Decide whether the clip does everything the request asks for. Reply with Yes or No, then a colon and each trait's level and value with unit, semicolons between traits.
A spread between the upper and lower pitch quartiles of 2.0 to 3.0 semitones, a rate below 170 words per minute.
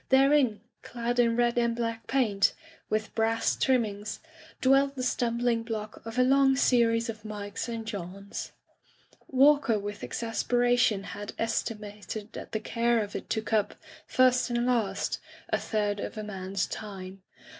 Yes: average, 2.7 semitones; average, 150 wpm